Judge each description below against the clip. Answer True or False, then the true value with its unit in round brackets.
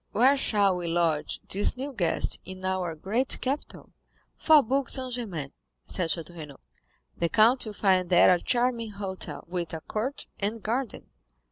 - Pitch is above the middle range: True (200 Hz)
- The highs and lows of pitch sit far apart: True (5.9 semitones)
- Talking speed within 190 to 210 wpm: False (155 wpm)